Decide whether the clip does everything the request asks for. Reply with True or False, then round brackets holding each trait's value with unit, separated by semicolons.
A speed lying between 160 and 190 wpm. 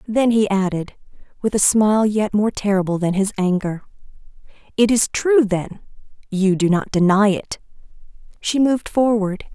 False (150 wpm)